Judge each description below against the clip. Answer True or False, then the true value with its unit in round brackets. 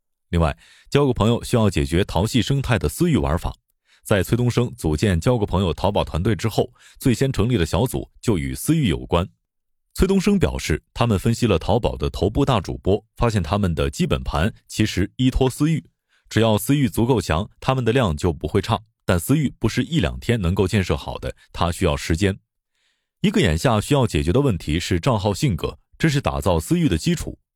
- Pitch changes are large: True (6.3 semitones)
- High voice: False (105 Hz)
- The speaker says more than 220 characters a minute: True (305 characters per minute)